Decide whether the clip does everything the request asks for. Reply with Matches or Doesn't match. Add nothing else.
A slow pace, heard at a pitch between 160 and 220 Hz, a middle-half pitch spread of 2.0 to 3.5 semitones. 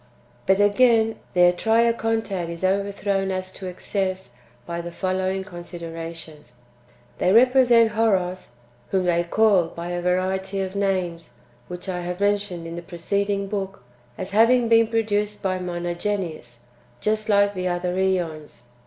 Doesn't match